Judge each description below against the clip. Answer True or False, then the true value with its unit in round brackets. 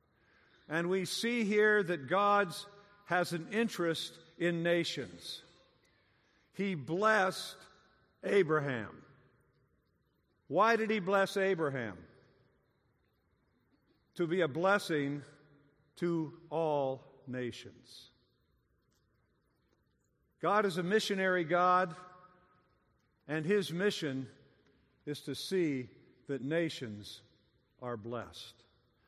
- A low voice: False (160 Hz)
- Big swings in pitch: True (6.4 semitones)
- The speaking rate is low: True (85 wpm)